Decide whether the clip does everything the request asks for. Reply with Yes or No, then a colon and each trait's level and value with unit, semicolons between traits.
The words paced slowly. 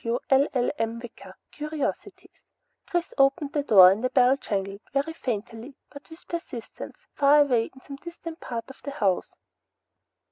No: average, 150 wpm